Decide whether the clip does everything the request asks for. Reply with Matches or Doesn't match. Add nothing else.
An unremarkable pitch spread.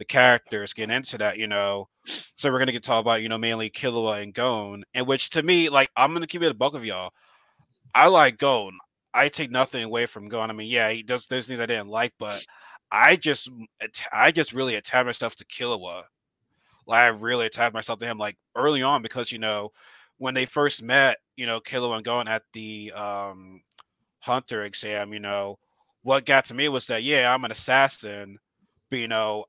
Matches